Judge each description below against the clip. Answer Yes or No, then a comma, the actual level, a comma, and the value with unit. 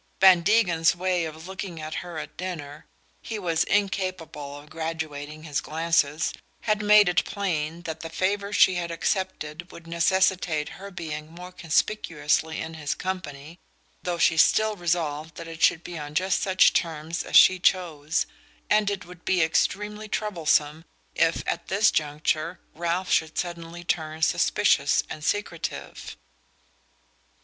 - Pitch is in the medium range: Yes, medium, 170 Hz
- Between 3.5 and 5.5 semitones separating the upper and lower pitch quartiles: No, average, 3.0 semitones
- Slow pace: No, average, 150 wpm